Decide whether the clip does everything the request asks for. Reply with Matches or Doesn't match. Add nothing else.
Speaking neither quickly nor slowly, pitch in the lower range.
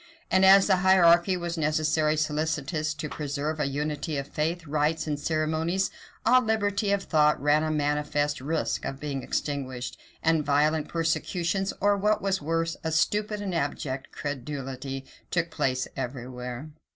Doesn't match